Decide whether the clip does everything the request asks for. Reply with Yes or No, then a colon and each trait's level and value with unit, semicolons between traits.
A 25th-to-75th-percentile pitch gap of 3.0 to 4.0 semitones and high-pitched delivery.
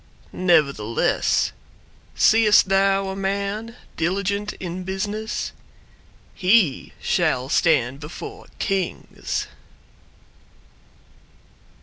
Yes: average, 3.6 semitones; high, 195 Hz